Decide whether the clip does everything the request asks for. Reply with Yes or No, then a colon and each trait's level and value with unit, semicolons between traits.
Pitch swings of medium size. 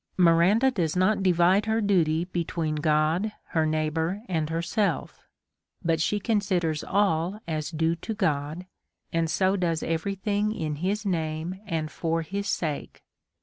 Yes: average, 3.8 semitones